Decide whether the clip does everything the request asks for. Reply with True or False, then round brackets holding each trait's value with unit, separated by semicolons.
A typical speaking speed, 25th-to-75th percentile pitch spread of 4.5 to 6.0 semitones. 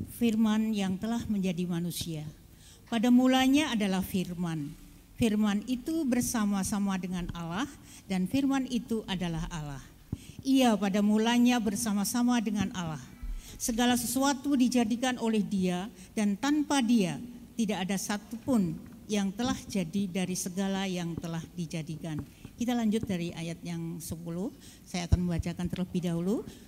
True (125 wpm; 5.0 semitones)